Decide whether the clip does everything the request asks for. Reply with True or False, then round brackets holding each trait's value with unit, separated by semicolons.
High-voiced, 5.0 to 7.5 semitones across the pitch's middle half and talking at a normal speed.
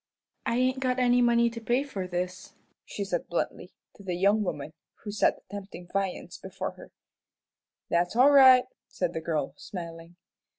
True (200 Hz; 5.5 semitones; 170 wpm)